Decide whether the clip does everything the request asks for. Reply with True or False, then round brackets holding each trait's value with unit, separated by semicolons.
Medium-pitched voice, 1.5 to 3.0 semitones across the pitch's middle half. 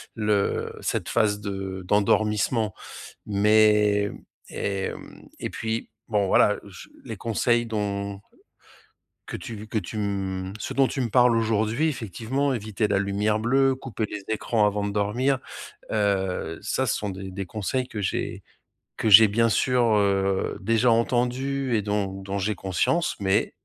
False (105 Hz; 2.7 semitones)